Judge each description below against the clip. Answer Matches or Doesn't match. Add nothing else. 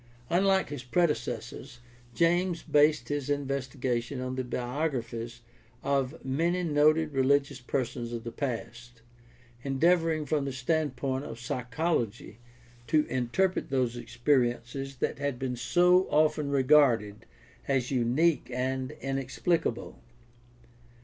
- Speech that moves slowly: Matches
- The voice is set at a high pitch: Doesn't match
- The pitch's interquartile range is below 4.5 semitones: Matches